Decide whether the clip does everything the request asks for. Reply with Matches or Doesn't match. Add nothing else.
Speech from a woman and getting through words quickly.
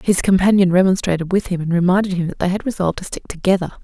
Matches